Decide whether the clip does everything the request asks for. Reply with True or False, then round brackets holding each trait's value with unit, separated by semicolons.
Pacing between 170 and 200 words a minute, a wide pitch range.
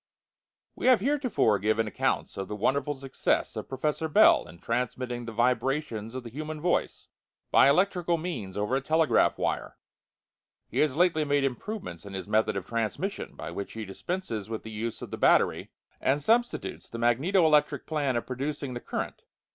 True (175 wpm; 5.8 semitones)